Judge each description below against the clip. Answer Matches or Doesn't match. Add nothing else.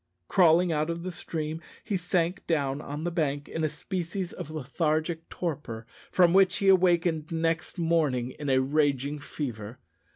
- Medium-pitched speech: Matches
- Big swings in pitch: Doesn't match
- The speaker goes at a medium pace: Matches